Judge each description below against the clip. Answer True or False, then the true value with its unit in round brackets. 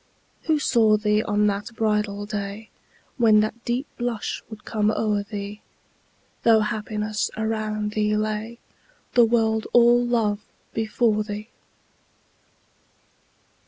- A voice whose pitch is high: True (215 Hz)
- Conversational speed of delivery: False (115 wpm)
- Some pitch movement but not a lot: False (1.3 semitones)